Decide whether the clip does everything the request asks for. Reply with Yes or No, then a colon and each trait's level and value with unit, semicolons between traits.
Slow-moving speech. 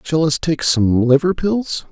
No: average, 190 wpm